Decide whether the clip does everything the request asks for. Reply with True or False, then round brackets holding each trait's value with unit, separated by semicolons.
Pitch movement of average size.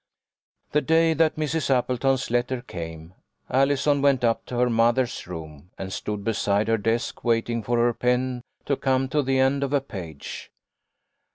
True (3.4 semitones)